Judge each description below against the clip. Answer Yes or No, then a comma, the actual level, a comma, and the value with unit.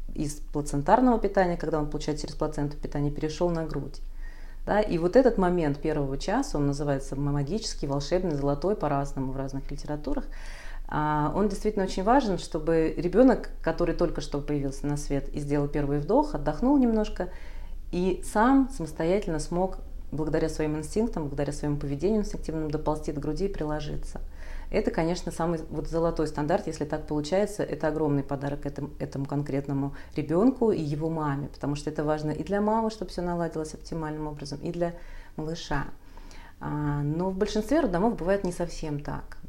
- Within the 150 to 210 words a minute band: Yes, fast, 160 wpm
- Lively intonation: No, average, 3.8 semitones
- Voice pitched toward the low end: No, medium, 155 Hz